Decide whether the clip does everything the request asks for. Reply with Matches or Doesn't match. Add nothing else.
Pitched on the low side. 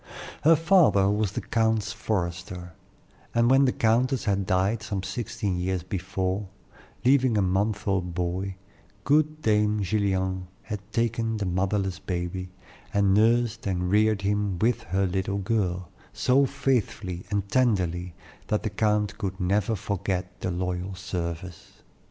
Matches